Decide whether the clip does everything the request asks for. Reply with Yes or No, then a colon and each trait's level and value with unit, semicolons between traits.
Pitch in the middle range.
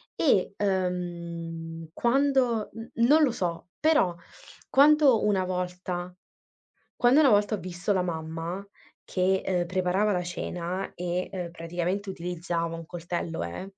Yes: medium, 180 Hz